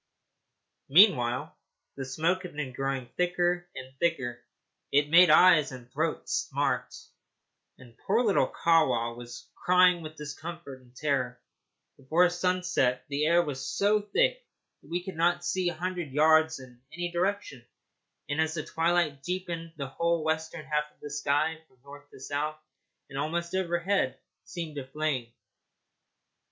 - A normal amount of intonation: Yes, average, 4.2 semitones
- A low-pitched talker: No, medium, 160 Hz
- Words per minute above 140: Yes, average, 150 wpm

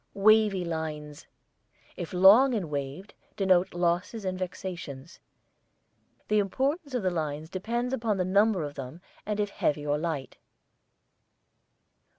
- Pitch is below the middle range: No, medium, 185 Hz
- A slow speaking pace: Yes, slow, 130 wpm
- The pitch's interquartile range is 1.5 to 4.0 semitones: No, average, 5.0 semitones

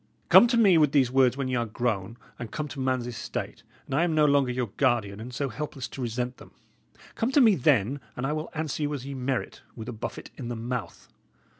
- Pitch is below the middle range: Yes, low, 130 Hz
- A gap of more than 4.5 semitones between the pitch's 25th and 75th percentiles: No, average, 3.7 semitones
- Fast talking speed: Yes, fast, 240 wpm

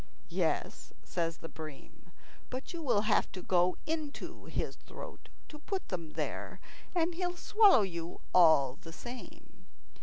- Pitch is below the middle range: No, high, 205 Hz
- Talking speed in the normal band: Yes, average, 145 wpm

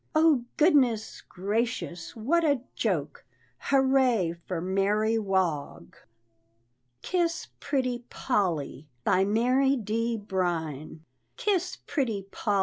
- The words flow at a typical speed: No, slow, 95 wpm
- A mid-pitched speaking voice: No, high, 225 Hz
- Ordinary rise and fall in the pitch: No, wide, 6.1 semitones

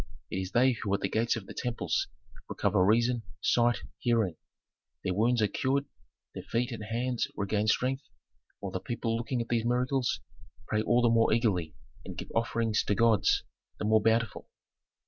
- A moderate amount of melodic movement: No, narrow, 2.3 semitones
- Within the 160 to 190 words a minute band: Yes, average, 175 wpm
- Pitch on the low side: Yes, low, 115 Hz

